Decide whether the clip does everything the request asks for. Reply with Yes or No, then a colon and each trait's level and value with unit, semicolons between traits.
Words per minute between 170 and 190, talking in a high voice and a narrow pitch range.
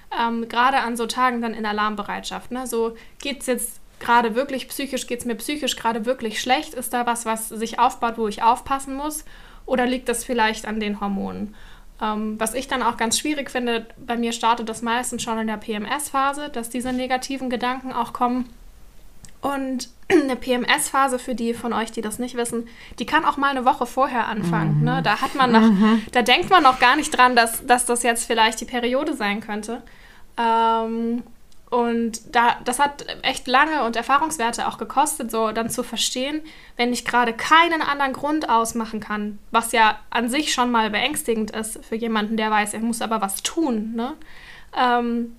Yes: average, 185 wpm; high, 235 Hz; narrow, 2.2 semitones